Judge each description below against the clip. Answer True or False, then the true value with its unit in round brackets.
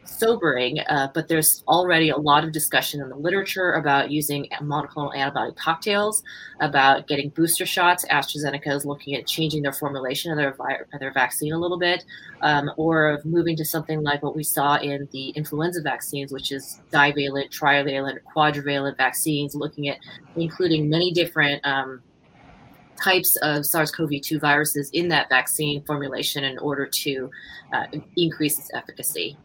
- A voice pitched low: False (150 Hz)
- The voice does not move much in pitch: True (2.3 semitones)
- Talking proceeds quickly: False (165 wpm)